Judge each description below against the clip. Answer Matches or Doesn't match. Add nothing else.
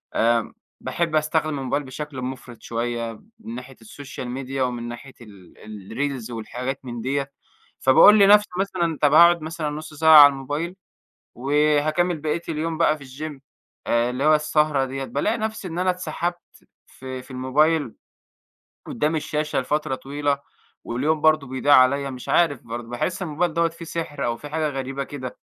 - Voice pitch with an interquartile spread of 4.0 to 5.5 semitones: Doesn't match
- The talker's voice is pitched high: Doesn't match